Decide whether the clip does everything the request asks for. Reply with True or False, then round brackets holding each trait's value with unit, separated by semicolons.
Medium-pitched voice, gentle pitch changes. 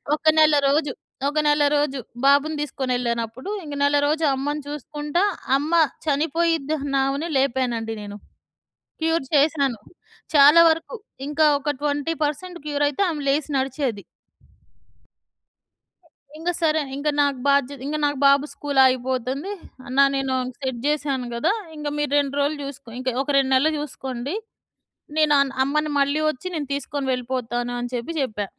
False (285 Hz; 2.3 semitones)